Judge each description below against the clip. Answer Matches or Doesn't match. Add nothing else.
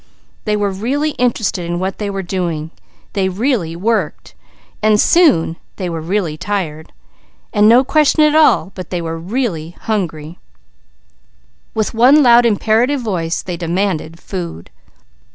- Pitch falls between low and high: Doesn't match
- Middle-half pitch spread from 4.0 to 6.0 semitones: Matches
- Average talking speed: Doesn't match